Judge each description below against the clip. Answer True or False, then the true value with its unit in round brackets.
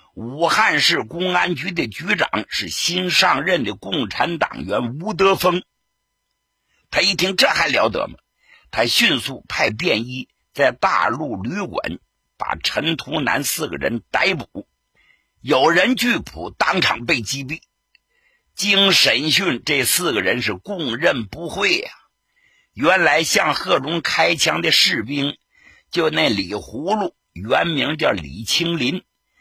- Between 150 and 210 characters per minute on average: True (190 characters per minute)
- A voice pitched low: False (180 Hz)